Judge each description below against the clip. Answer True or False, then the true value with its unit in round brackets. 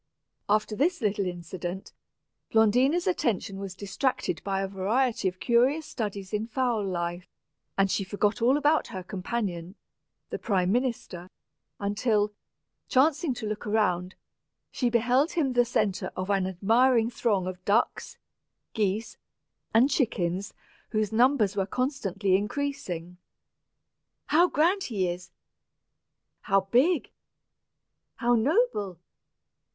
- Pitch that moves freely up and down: False (4.7 semitones)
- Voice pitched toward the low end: False (210 Hz)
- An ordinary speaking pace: False (120 wpm)